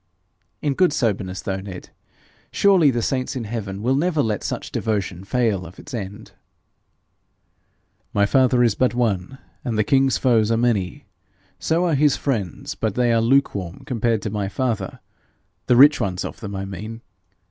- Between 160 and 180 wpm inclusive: Yes, average, 170 wpm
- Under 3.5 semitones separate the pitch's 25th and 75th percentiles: No, average, 4.7 semitones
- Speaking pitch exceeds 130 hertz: No, low, 115 Hz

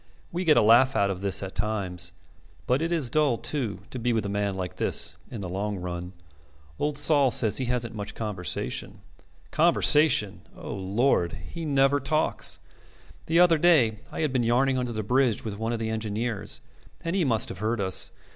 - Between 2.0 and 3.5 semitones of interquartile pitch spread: No, average, 5.3 semitones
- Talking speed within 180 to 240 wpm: Yes, average, 195 wpm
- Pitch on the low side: Yes, low, 115 Hz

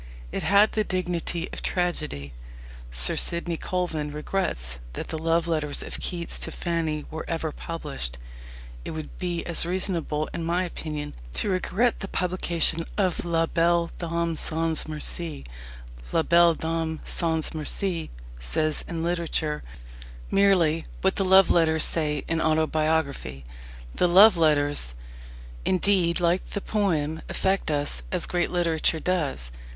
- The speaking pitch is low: No, medium, 165 Hz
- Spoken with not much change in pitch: Yes, narrow, 2.3 semitones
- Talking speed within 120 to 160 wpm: Yes, slow, 135 wpm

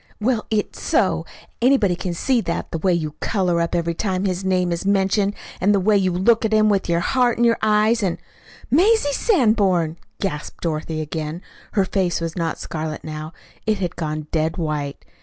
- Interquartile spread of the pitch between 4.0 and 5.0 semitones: Yes, average, 4.3 semitones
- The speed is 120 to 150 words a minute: No, average, 195 wpm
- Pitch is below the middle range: No, medium, 185 Hz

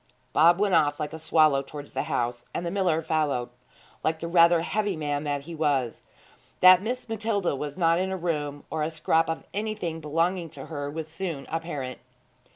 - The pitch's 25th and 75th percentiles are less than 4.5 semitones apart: Yes, average, 3.1 semitones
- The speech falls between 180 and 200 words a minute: Yes, average, 190 wpm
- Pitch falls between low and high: Yes, medium, 160 Hz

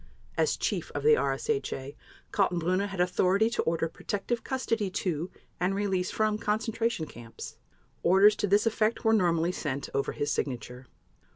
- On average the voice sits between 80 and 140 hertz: No, high, 190 Hz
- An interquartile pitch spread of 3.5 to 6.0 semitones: Yes, average, 4.7 semitones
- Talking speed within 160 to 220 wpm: No, average, 150 wpm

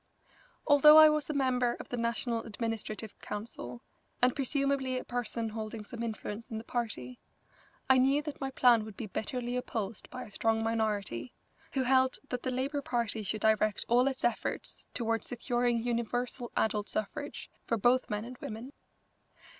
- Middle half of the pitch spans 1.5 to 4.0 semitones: Yes, average, 2.8 semitones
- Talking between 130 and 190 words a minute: Yes, average, 165 wpm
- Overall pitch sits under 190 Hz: No, high, 235 Hz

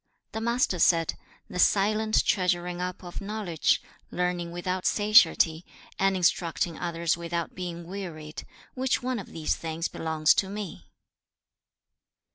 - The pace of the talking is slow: Yes, slow, 125 wpm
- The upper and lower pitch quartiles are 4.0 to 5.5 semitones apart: No, average, 3.0 semitones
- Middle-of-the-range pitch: Yes, medium, 180 Hz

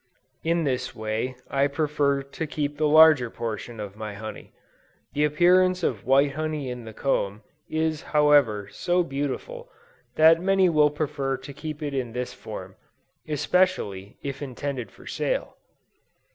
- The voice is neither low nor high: Yes, medium, 145 Hz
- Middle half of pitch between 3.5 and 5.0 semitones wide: Yes, average, 4.1 semitones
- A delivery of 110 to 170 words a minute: Yes, average, 145 wpm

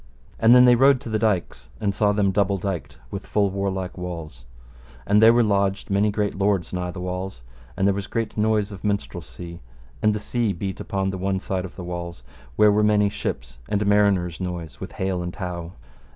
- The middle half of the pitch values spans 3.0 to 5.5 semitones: No, narrow, 2.6 semitones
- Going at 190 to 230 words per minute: Yes, fast, 205 wpm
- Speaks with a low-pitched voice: Yes, low, 100 Hz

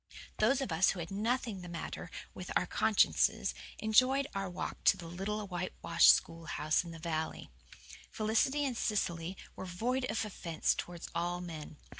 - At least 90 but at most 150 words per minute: No, average, 160 wpm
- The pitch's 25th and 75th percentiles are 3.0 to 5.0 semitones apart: Yes, average, 4.5 semitones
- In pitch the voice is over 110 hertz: Yes, medium, 185 Hz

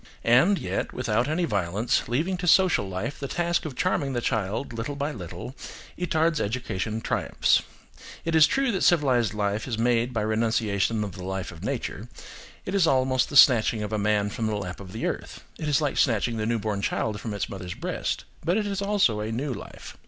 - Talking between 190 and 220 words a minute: Yes, average, 200 wpm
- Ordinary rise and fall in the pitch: No, wide, 5.9 semitones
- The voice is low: Yes, low, 120 Hz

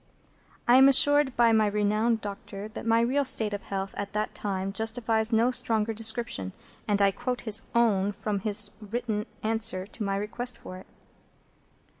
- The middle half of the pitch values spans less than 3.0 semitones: Yes, narrow, 2.5 semitones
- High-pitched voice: Yes, high, 220 Hz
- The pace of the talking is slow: No, average, 170 wpm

